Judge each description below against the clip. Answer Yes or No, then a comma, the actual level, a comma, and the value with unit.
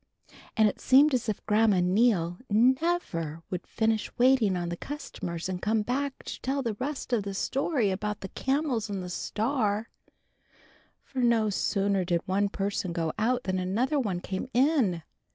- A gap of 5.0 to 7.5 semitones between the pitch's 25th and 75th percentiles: Yes, average, 5.3 semitones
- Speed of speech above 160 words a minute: Yes, average, 170 wpm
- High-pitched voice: Yes, high, 215 Hz